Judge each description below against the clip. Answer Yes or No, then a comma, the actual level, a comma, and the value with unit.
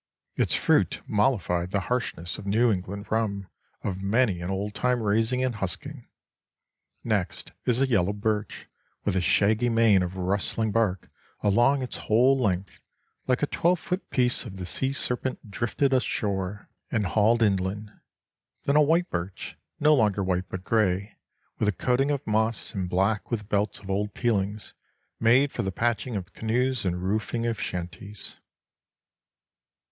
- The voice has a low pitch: Yes, low, 105 Hz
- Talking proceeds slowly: No, average, 160 wpm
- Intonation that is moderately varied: Yes, average, 3.9 semitones